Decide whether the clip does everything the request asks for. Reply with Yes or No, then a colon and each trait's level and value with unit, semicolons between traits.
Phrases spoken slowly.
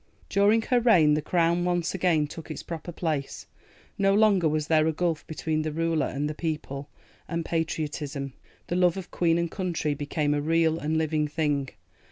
No: average, 185 wpm